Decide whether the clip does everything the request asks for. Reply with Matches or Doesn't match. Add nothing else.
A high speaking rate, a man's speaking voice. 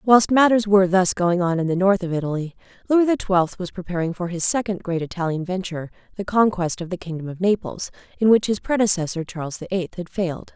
Doesn't match